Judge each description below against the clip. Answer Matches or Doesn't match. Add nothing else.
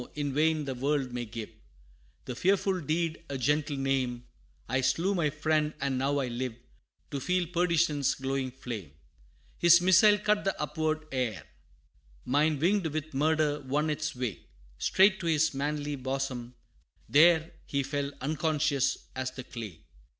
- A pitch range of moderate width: Matches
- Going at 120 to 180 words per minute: Matches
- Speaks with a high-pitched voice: Doesn't match